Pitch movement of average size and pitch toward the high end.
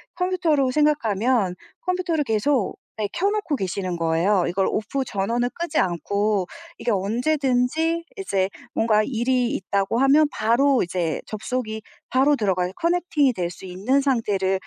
No: wide, 6.8 semitones; high, 235 Hz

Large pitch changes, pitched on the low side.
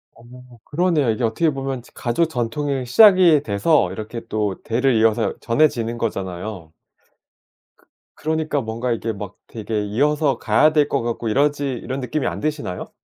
No: average, 5.0 semitones; low, 125 Hz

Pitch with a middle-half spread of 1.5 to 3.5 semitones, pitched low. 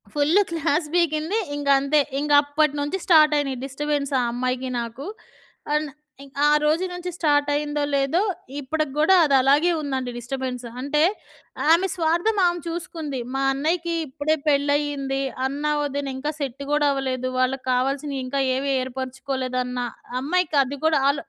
No: narrow, 2.4 semitones; very high, 285 Hz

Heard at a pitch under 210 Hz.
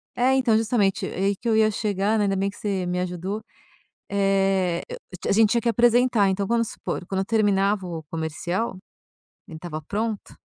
Yes: high, 200 Hz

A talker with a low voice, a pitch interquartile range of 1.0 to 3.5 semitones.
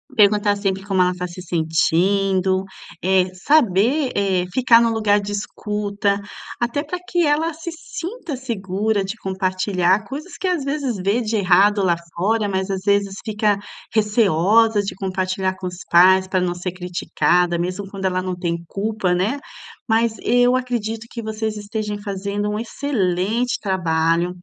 No: high, 200 Hz; average, 3.2 semitones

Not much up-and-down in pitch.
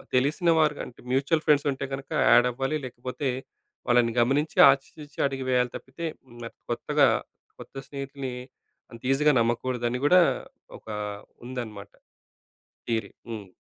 No: average, 3.0 semitones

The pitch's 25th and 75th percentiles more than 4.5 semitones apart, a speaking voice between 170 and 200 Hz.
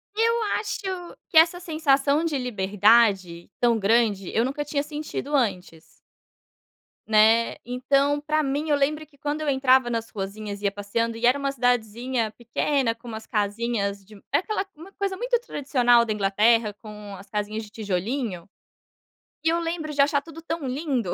No: wide, 5.5 semitones; high, 245 Hz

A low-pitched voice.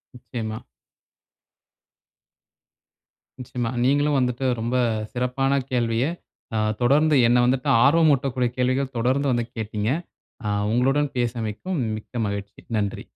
Yes: low, 125 Hz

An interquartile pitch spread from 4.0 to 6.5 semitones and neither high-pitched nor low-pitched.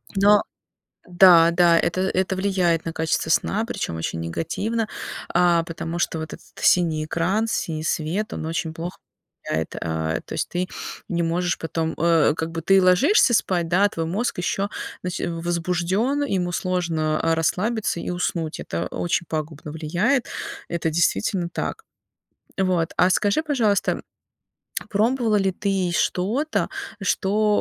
No: average, 3.3 semitones; medium, 175 Hz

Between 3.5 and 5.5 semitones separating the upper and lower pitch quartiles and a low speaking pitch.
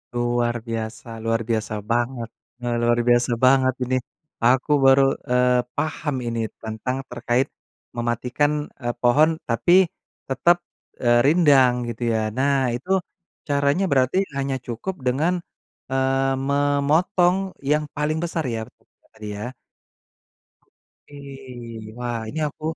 No: average, 3.1 semitones; low, 130 Hz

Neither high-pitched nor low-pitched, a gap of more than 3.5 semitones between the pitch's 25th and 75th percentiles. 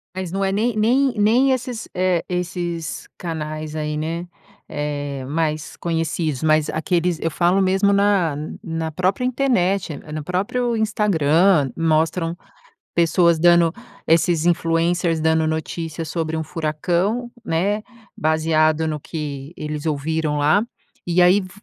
No: medium, 165 Hz; average, 3.2 semitones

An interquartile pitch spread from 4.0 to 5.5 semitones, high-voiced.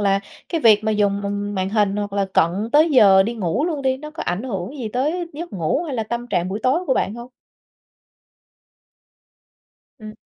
Yes: average, 4.9 semitones; high, 220 Hz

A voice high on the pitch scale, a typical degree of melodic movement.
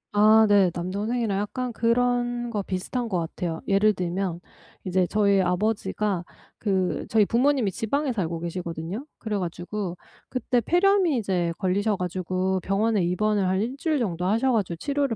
Yes: high, 205 Hz; average, 4.3 semitones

